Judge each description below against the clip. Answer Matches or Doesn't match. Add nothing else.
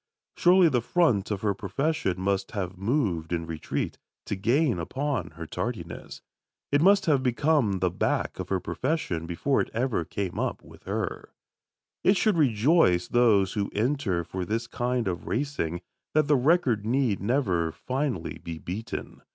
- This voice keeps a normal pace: Matches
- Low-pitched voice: Matches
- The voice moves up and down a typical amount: Doesn't match